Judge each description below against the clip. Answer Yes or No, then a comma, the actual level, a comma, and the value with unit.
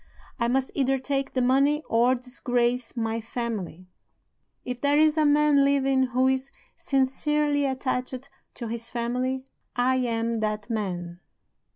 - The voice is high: Yes, very high, 255 Hz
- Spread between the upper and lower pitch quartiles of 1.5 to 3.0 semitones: Yes, narrow, 2.6 semitones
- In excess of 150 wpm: No, average, 140 wpm